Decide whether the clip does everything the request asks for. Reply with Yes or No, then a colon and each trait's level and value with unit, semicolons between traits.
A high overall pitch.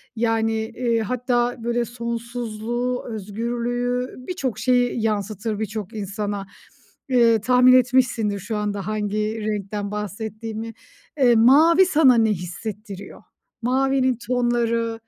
Yes: high, 230 Hz